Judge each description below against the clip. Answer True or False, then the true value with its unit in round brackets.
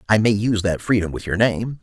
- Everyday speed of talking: False (265 wpm)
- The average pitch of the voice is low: True (105 Hz)